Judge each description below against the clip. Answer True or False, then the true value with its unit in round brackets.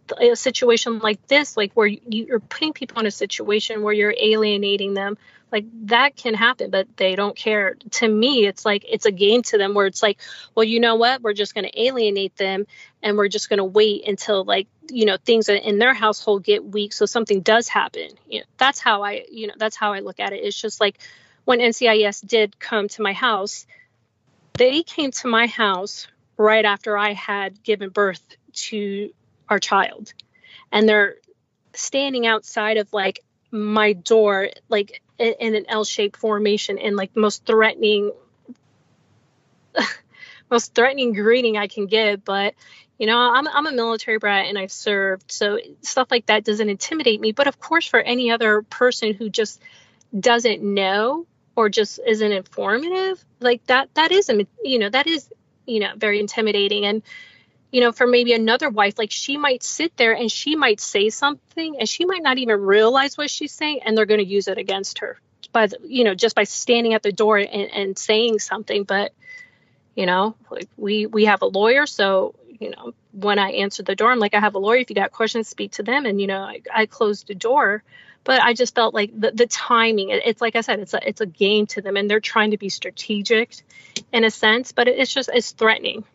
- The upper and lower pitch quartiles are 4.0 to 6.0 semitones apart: False (2.7 semitones)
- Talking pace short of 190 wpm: False (200 wpm)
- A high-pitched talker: True (220 Hz)